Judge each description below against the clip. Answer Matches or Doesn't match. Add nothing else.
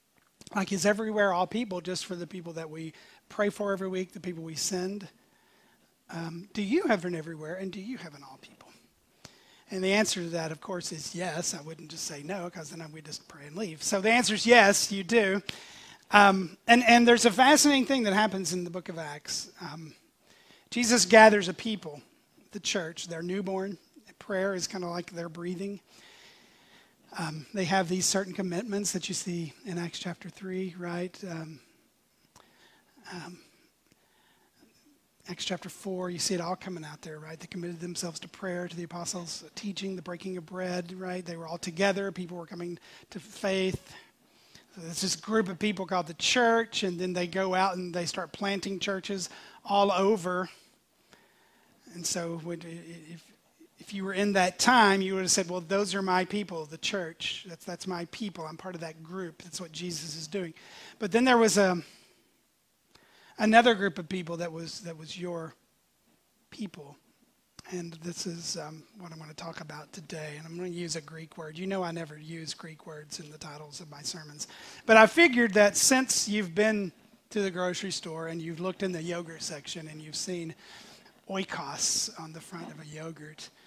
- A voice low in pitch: Doesn't match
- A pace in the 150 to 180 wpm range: Doesn't match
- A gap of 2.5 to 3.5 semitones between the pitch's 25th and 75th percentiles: Matches